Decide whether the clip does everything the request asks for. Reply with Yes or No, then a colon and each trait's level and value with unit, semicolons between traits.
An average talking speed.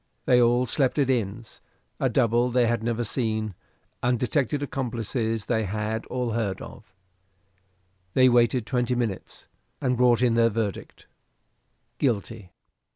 No: slow, 130 wpm